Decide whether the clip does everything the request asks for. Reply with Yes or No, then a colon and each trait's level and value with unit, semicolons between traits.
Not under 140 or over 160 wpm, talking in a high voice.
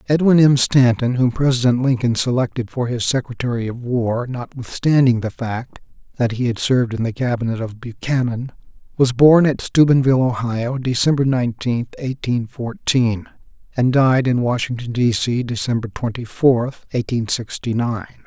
No: average, 150 wpm; low, 125 Hz